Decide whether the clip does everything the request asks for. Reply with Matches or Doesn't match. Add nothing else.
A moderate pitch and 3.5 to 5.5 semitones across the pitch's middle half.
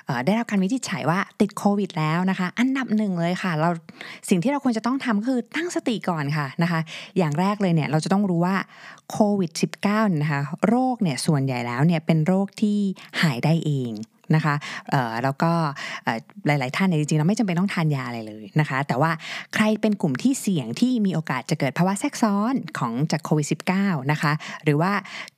Matches